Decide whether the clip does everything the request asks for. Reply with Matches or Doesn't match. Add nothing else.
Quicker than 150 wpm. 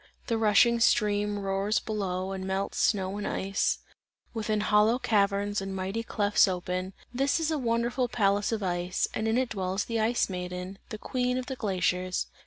Matches